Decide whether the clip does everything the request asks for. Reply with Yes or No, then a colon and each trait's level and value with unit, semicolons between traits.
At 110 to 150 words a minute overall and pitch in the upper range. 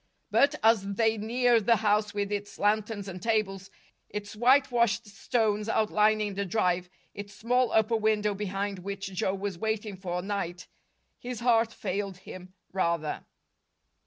Yes: average, 140 wpm; high, 205 Hz